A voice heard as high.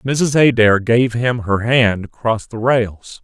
No: low, 115 Hz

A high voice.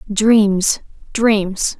Yes: high, 205 Hz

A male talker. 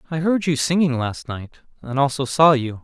Yes: male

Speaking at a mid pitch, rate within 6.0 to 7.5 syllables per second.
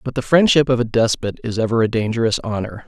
No: low, 115 Hz; 6.3 syllables/s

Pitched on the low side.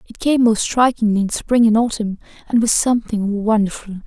No: high, 220 Hz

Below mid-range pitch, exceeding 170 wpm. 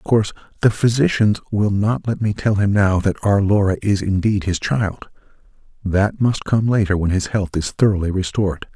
Yes: low, 100 Hz; average, 185 wpm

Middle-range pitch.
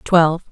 Yes: medium, 165 Hz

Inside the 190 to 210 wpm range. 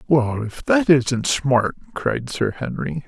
No: average, 155 wpm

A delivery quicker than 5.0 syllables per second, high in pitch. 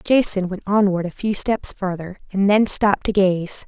No: 4.6 syllables/s; high, 195 Hz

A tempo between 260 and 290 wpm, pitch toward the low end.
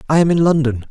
No: fast, 265 wpm; medium, 145 Hz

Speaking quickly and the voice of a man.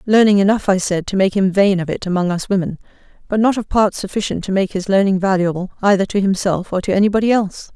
No: fast, 240 wpm; female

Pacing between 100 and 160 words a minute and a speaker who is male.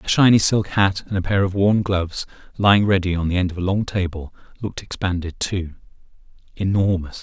No: average, 190 wpm; male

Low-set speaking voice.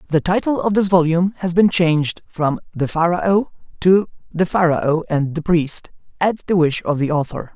No: medium, 170 Hz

